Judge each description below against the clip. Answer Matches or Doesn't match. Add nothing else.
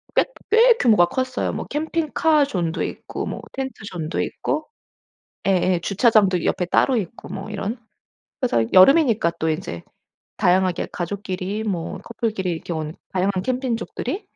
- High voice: Matches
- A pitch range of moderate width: Doesn't match